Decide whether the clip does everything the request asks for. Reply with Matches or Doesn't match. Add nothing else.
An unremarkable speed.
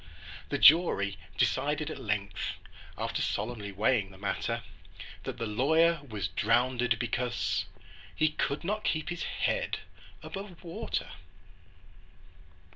Doesn't match